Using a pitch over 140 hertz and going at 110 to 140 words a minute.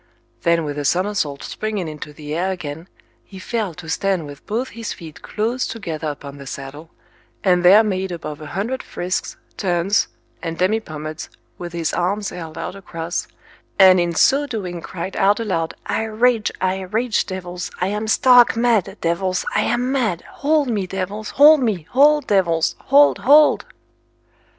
No: medium, 185 Hz; average, 165 wpm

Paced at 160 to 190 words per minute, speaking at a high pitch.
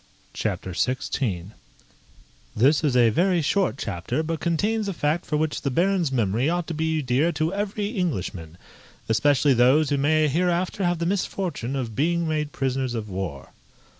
No: average, 165 wpm; medium, 150 Hz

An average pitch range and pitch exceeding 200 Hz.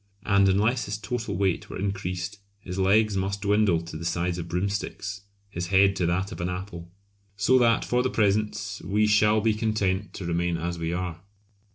No: average, 3.1 semitones; low, 100 Hz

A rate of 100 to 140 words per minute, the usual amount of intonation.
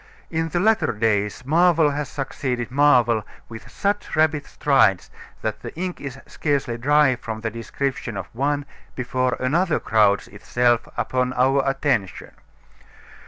Yes: slow, 135 wpm; average, 4.1 semitones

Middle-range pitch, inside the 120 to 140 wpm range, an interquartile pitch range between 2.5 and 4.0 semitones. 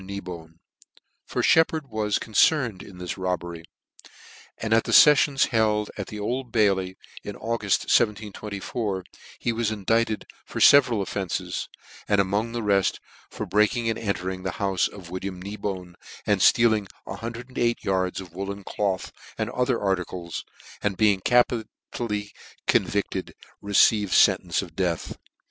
No: low, 105 Hz; slow, 135 wpm; average, 3.2 semitones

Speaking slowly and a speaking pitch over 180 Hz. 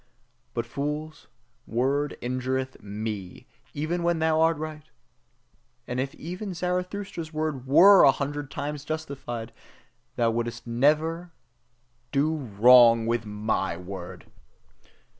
No: slow, 115 wpm; medium, 140 Hz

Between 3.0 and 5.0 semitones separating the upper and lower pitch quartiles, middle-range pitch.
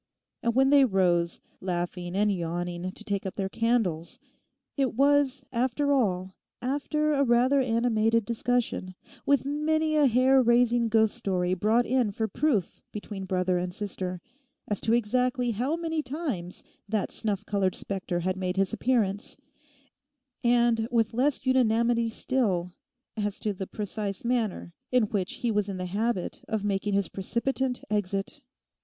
No: average, 4.7 semitones; high, 220 Hz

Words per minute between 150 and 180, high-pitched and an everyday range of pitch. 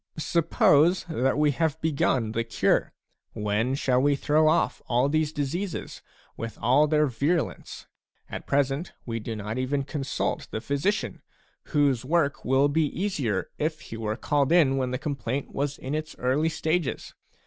No: average, 160 wpm; medium, 140 Hz; average, 3.6 semitones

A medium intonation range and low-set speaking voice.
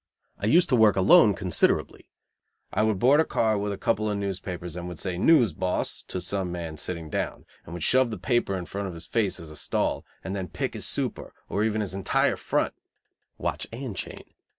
Yes: average, 3.6 semitones; low, 100 Hz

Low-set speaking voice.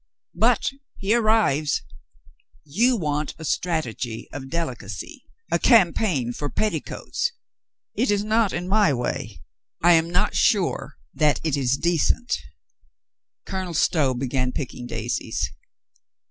No: medium, 160 Hz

